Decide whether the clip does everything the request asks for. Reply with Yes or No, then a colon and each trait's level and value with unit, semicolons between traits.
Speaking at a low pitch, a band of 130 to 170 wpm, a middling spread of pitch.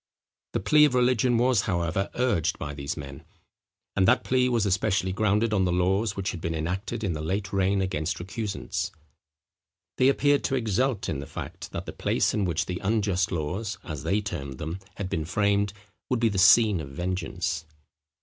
No: very low, 95 Hz; average, 190 wpm; average, 4.4 semitones